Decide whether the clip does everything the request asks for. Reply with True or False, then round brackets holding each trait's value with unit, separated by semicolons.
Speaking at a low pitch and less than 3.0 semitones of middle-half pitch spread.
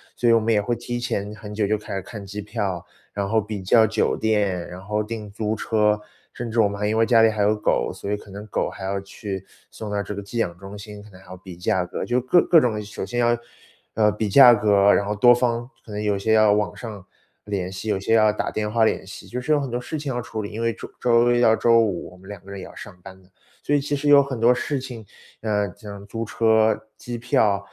True (105 Hz; 2.5 semitones)